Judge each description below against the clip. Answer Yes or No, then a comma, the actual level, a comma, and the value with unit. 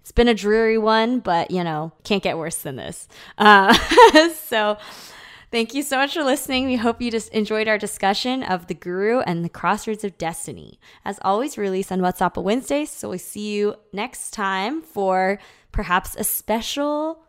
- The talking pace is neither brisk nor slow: Yes, average, 185 wpm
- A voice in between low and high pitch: No, high, 215 Hz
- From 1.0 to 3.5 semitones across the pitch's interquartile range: No, average, 4.7 semitones